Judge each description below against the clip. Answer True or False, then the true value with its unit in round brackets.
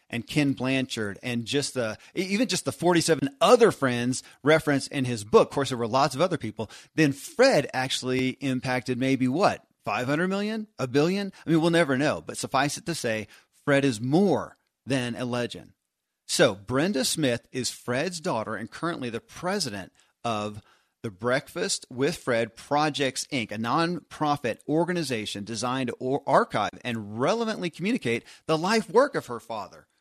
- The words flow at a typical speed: True (165 wpm)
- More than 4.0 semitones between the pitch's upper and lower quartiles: True (4.8 semitones)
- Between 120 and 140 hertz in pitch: True (135 Hz)